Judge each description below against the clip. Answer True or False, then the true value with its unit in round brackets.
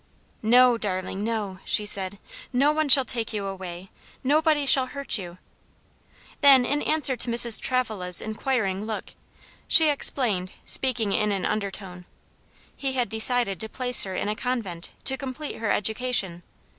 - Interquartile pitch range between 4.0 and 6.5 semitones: True (4.8 semitones)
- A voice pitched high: True (225 Hz)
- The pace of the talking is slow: False (150 wpm)